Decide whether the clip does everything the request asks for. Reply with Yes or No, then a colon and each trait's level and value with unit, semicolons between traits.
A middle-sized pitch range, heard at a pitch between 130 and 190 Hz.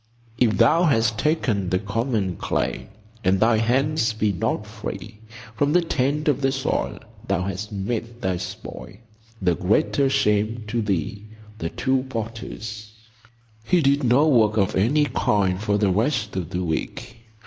No: average, 4.3 semitones; low, 110 Hz